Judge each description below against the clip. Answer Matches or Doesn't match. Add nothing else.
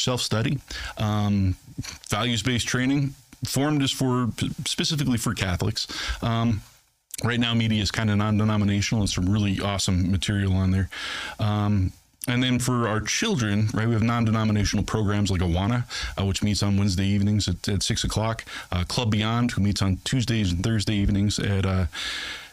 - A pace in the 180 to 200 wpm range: Doesn't match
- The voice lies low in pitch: Matches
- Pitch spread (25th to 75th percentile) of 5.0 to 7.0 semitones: Doesn't match